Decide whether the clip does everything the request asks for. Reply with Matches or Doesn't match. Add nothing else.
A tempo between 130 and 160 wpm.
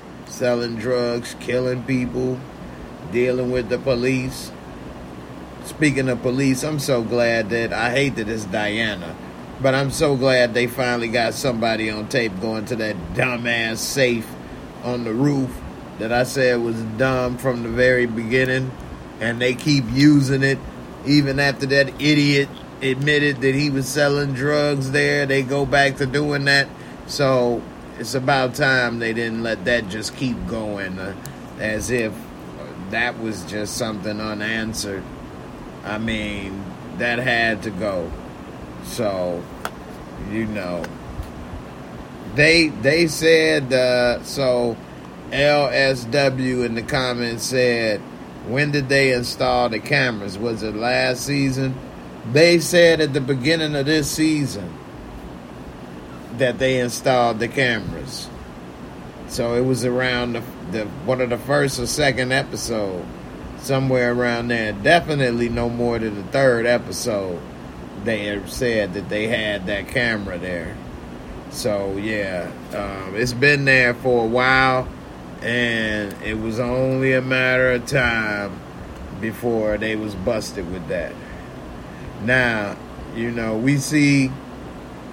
Matches